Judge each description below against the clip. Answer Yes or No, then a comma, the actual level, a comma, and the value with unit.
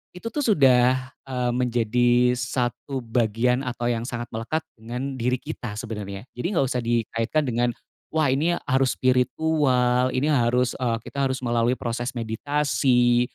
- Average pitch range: No, narrow, 1.9 semitones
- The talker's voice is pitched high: No, low, 125 Hz